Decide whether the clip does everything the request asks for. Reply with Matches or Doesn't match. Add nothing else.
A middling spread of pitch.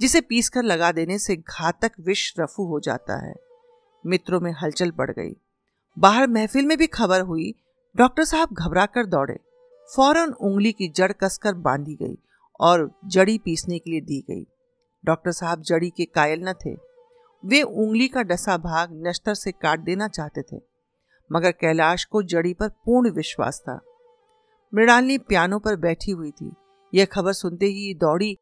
Doesn't match